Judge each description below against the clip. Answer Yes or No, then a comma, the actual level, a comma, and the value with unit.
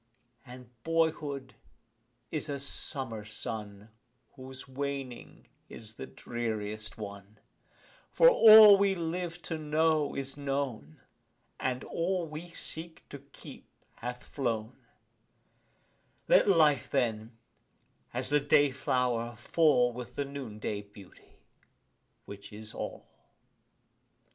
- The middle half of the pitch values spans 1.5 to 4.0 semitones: No, wide, 5.5 semitones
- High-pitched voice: No, low, 130 Hz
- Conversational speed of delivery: No, slow, 110 wpm